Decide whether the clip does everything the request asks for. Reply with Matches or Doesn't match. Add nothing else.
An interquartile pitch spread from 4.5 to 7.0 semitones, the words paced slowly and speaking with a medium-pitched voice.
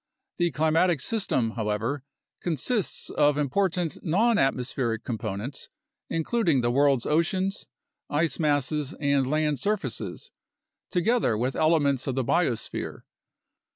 Matches